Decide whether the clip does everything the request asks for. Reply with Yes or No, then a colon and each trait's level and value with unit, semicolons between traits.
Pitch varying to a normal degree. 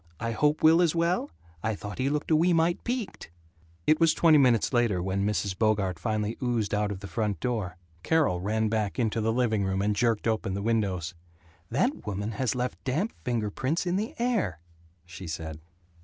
No: wide, 6.8 semitones